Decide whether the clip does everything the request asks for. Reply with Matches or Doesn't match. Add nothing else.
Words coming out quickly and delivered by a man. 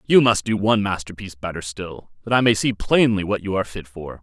Matches